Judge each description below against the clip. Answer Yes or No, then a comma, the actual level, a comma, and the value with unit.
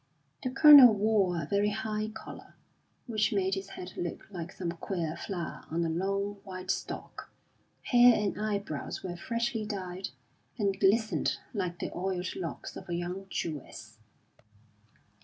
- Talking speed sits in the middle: Yes, average, 145 wpm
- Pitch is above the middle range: Yes, high, 195 Hz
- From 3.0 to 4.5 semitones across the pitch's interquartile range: Yes, average, 3.4 semitones